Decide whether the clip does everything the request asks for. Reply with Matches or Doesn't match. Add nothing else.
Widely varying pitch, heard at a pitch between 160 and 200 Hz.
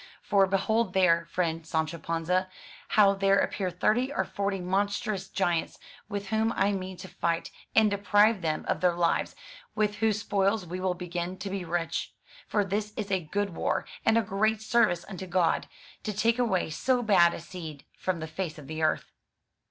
Doesn't match